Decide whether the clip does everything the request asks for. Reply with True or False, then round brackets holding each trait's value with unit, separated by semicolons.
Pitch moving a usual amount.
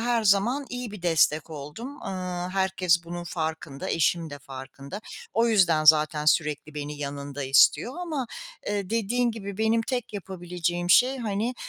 False (6.4 semitones)